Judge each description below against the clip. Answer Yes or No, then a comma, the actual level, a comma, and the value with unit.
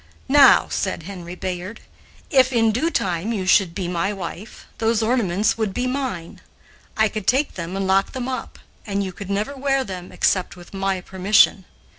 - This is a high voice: Yes, high, 200 Hz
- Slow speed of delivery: No, average, 180 wpm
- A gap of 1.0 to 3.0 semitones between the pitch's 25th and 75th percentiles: No, average, 4.1 semitones